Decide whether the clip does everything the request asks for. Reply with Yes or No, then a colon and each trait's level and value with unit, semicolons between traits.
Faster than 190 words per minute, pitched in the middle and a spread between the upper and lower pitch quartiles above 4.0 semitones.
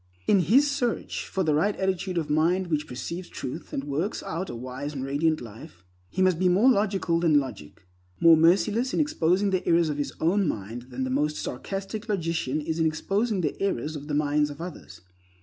Yes: average, 200 wpm; medium, 165 Hz; average, 4.7 semitones